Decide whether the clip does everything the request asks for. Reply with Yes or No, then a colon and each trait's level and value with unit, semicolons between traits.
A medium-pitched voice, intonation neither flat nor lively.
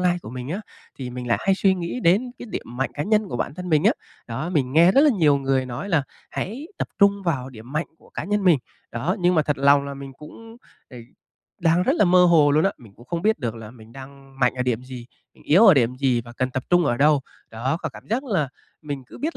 No: medium, 150 Hz; wide, 6.1 semitones